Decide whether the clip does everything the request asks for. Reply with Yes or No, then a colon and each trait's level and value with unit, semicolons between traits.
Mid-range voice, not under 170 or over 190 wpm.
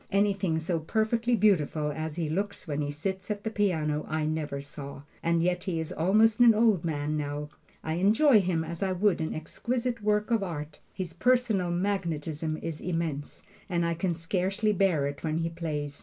Yes: medium, 170 Hz; average, 185 wpm